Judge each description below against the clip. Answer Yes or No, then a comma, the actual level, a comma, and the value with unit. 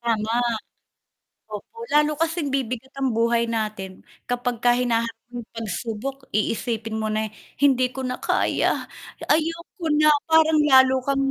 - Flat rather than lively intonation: No, average, 3.5 semitones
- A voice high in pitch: Yes, high, 245 Hz